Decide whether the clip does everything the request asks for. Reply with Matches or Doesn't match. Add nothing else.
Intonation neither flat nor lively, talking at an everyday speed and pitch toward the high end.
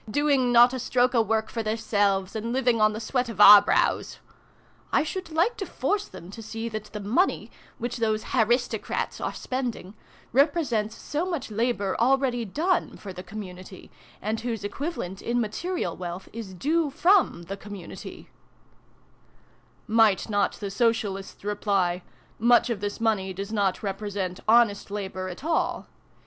Matches